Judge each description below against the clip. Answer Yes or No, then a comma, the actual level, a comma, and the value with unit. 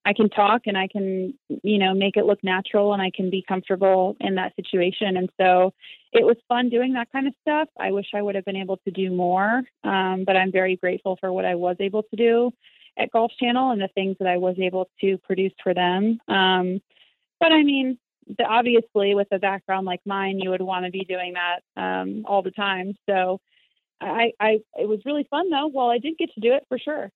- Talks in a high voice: Yes, high, 195 Hz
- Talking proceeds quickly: Yes, fast, 230 wpm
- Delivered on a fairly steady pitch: No, average, 3.8 semitones